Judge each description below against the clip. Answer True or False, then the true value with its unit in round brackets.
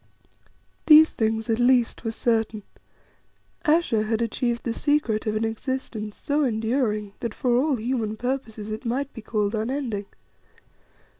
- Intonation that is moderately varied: True (3.1 semitones)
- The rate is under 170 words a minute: True (140 wpm)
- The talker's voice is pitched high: True (230 Hz)